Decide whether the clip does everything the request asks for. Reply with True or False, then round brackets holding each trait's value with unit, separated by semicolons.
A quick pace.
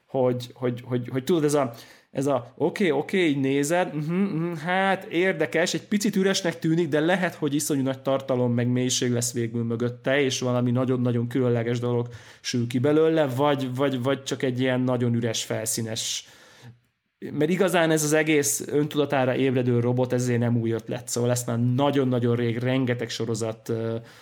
True (175 wpm)